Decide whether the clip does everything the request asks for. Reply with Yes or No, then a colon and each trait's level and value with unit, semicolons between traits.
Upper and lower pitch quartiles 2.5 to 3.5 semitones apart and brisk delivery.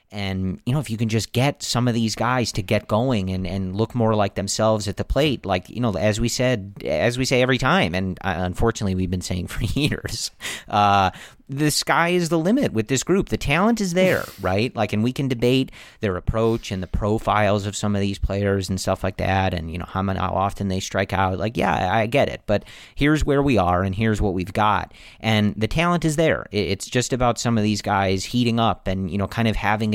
No: average, 4.2 semitones; fast, 240 wpm